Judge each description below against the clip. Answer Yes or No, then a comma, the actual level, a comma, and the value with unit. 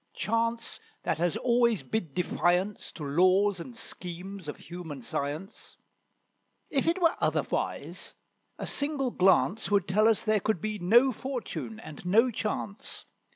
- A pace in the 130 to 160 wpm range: Yes, average, 140 wpm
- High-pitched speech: Yes, high, 205 Hz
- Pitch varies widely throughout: No, average, 4.5 semitones